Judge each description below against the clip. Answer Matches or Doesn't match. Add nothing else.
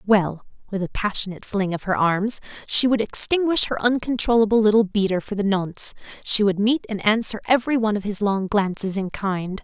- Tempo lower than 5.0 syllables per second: Matches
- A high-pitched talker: Matches